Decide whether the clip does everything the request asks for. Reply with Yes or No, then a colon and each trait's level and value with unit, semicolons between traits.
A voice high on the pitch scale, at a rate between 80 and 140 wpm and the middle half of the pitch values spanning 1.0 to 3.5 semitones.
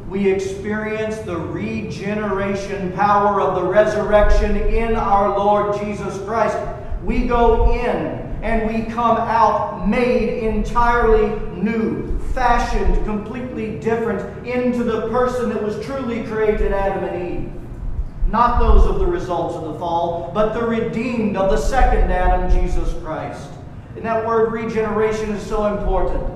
Yes: high, 215 Hz; slow, 135 wpm; narrow, 2.6 semitones